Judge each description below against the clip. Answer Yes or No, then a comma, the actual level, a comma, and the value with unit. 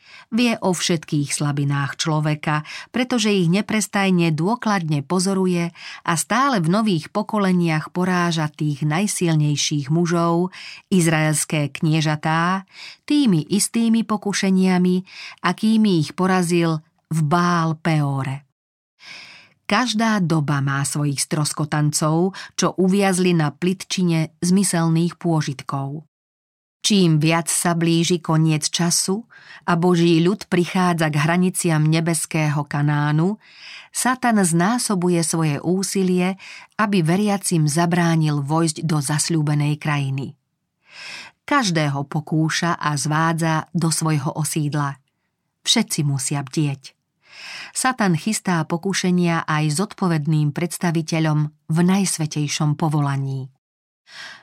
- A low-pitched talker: No, medium, 170 Hz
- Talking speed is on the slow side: Yes, slow, 95 wpm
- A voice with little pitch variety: No, average, 3.4 semitones